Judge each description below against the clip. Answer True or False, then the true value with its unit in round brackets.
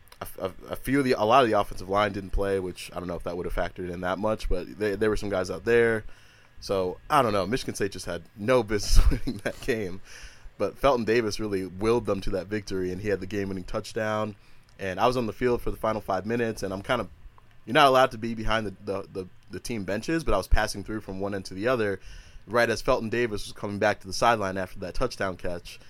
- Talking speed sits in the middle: False (260 wpm)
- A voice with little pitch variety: False (3.1 semitones)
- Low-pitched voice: True (105 Hz)